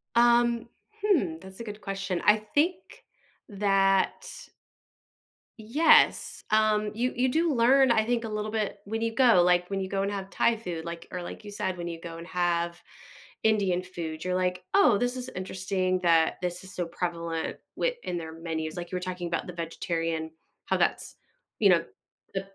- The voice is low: No, high, 190 Hz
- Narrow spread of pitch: No, average, 4.3 semitones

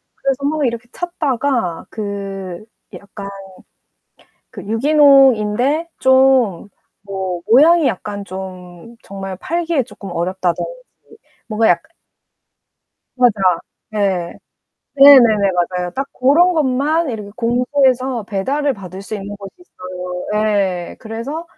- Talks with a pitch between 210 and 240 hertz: Yes, high, 225 Hz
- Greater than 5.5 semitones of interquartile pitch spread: Yes, wide, 6.1 semitones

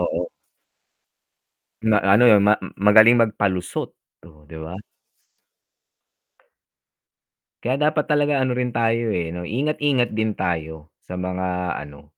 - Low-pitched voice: Yes, low, 105 Hz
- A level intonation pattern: No, wide, 5.6 semitones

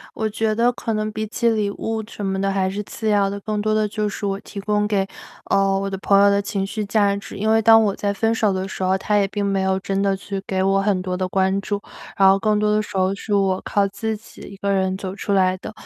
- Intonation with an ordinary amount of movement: No, narrow, 1.6 semitones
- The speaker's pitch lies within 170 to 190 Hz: No, high, 200 Hz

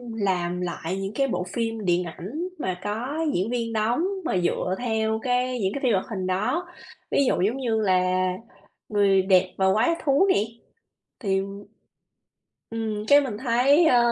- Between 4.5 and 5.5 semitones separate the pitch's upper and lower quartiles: Yes, average, 4.8 semitones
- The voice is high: Yes, high, 215 Hz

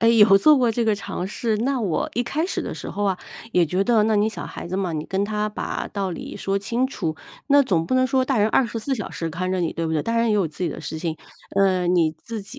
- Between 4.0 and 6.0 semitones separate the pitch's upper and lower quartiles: Yes, average, 4.4 semitones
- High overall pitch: Yes, high, 205 Hz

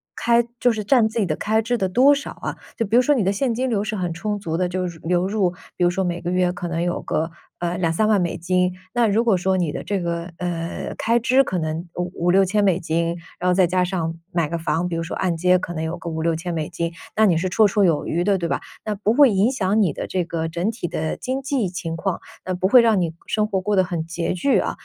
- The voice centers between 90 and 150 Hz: No, medium, 185 Hz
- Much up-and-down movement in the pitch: No, average, 3.9 semitones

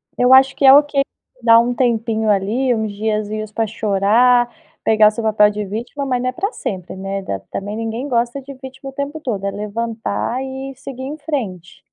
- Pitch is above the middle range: Yes, high, 230 Hz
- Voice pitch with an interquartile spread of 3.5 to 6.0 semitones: Yes, average, 3.9 semitones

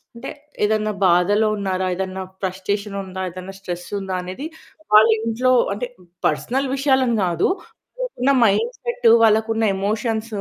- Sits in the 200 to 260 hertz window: Yes, high, 210 Hz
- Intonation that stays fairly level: No, average, 3.5 semitones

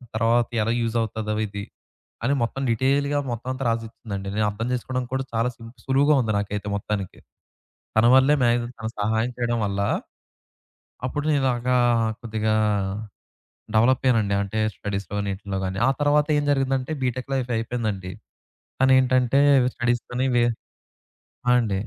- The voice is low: Yes, low, 115 Hz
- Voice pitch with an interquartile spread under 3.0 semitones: No, average, 3.3 semitones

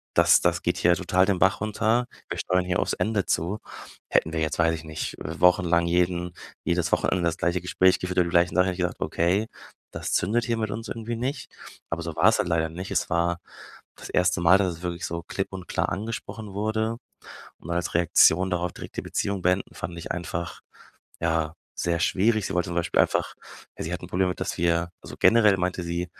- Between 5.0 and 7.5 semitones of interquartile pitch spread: No, narrow, 2.4 semitones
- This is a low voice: Yes, very low, 90 Hz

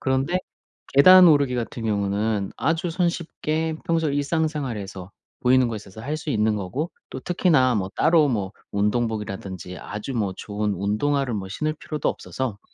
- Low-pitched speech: Yes, low, 125 Hz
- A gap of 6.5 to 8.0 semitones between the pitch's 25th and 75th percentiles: Yes, wide, 6.9 semitones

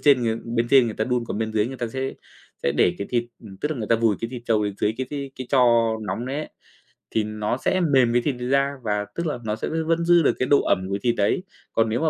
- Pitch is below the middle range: Yes, low, 120 Hz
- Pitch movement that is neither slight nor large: Yes, average, 3.5 semitones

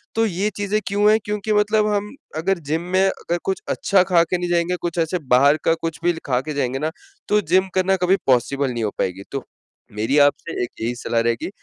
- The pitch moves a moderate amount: No, wide, 5.9 semitones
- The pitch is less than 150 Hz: No, medium, 175 Hz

